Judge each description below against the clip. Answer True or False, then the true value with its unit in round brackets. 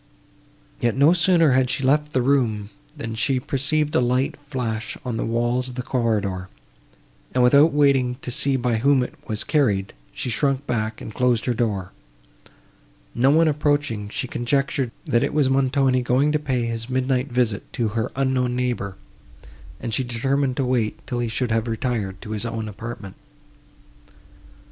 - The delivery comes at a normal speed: True (170 wpm)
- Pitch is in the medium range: False (125 Hz)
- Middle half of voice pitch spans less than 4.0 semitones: True (3.2 semitones)